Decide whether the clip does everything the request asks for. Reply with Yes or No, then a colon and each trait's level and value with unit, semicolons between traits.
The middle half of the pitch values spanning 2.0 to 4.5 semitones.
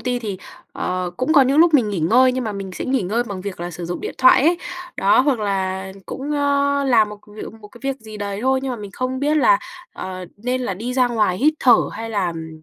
No: average, 5.1 semitones